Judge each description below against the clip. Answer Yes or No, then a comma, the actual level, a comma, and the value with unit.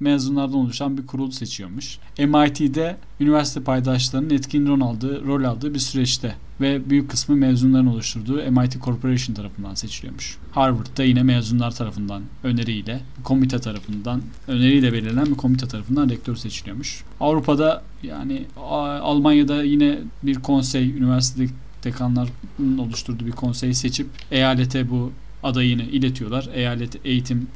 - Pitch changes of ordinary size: No, narrow, 2.2 semitones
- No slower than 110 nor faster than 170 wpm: Yes, average, 120 wpm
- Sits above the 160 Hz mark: No, low, 130 Hz